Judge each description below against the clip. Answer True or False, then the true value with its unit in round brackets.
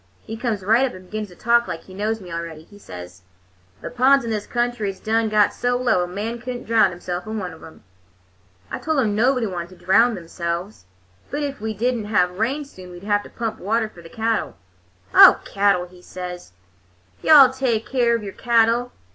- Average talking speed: False (220 wpm)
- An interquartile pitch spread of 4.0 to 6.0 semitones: True (4.6 semitones)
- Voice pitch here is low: False (215 Hz)